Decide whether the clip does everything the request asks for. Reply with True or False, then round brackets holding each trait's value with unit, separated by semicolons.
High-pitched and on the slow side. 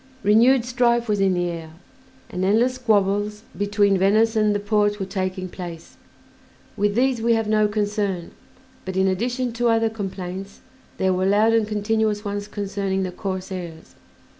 False (205 Hz; 160 wpm)